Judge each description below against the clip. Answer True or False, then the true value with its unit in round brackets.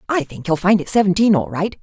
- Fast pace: True (265 wpm)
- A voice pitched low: False (190 Hz)